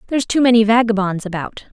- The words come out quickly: No, average, 170 wpm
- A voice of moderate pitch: No, high, 220 Hz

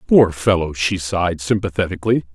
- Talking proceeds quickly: No, slow, 130 wpm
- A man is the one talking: Yes, male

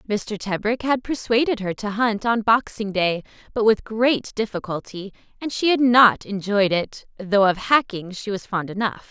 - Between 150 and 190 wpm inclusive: Yes, average, 180 wpm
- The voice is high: Yes, high, 210 Hz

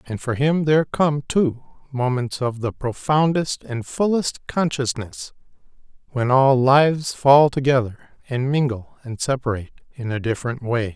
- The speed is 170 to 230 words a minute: No, average, 140 wpm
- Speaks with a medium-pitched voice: No, low, 130 Hz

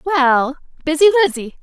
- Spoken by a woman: Yes, female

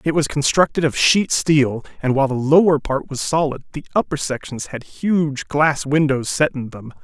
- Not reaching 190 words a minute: No, average, 195 wpm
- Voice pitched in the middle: Yes, medium, 145 Hz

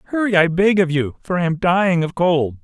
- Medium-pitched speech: Yes, medium, 175 Hz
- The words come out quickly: Yes, fast, 250 wpm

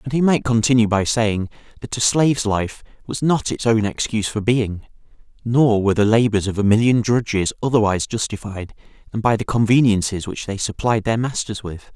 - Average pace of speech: Yes, average, 185 wpm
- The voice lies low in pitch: Yes, low, 110 Hz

